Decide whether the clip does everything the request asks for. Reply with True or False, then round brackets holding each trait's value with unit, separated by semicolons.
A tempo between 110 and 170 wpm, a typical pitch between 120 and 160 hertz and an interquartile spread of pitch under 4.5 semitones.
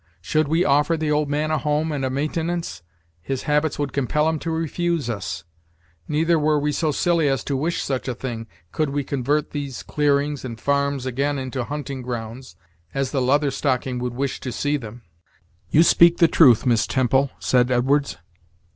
False (185 wpm; 140 Hz; 2.8 semitones)